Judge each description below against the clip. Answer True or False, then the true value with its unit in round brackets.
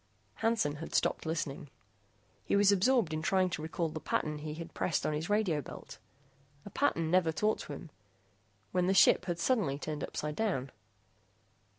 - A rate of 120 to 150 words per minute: False (170 wpm)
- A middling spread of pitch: True (4.5 semitones)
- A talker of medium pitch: True (165 Hz)